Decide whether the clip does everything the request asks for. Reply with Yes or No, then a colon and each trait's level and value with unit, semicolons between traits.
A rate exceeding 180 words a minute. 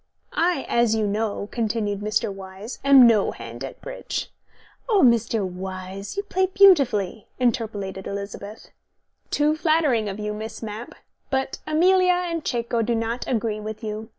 No: average, 150 wpm